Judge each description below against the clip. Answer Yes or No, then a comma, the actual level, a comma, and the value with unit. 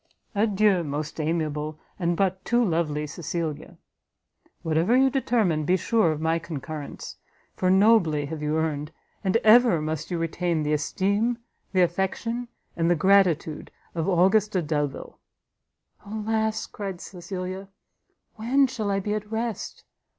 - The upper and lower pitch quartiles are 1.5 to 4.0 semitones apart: No, average, 5.1 semitones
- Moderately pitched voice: Yes, medium, 180 Hz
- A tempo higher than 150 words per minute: No, slow, 135 wpm